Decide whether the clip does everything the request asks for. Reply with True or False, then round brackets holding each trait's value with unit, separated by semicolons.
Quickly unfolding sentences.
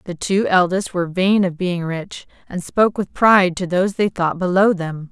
True (210 wpm)